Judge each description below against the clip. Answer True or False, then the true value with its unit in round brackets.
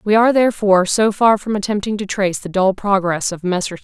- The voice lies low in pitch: False (200 Hz)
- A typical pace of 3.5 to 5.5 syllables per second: False (5.9 syllables/s)